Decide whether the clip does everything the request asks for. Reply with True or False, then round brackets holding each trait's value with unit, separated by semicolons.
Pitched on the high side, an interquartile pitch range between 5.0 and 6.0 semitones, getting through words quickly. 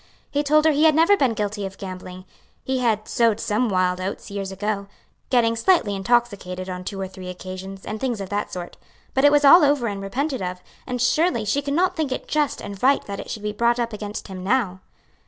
True (215 Hz; 5.5 semitones; 230 wpm)